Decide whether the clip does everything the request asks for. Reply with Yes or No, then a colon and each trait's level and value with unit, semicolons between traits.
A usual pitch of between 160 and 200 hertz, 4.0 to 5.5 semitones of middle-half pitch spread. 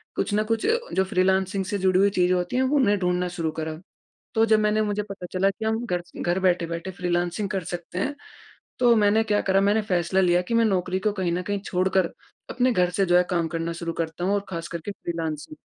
No: medium, 185 Hz; average, 2.8 semitones